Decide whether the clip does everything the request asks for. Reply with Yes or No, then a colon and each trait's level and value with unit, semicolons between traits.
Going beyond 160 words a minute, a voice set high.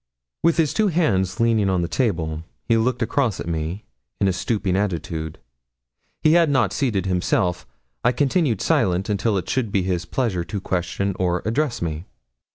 No: average, 170 wpm; low, 100 Hz